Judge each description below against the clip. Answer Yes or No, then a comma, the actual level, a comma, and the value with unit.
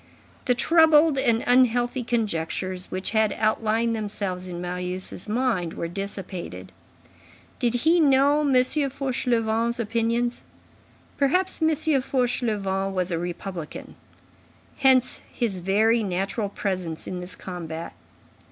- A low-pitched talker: No, high, 225 Hz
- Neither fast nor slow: No, slow, 110 wpm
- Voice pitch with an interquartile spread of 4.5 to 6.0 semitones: Yes, wide, 5.4 semitones